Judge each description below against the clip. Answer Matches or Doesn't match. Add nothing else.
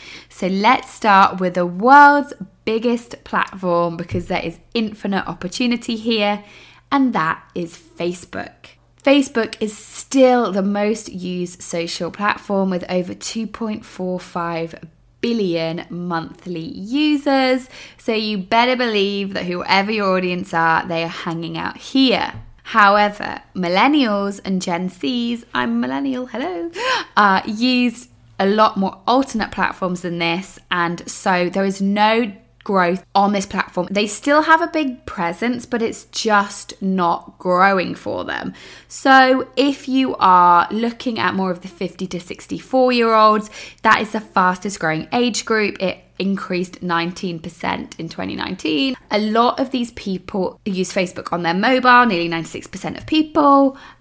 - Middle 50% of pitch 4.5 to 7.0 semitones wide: Matches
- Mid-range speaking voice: Doesn't match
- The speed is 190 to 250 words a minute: Doesn't match